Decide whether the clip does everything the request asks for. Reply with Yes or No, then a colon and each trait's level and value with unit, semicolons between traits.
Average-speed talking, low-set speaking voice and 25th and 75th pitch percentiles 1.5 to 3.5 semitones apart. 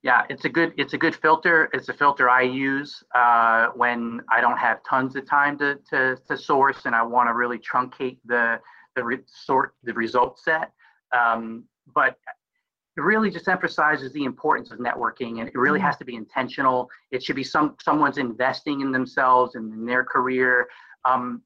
Yes: average, 190 wpm; low, 130 Hz; average, 2.8 semitones